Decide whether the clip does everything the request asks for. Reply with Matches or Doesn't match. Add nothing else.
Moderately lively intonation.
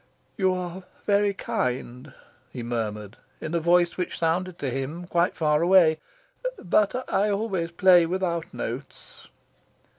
Matches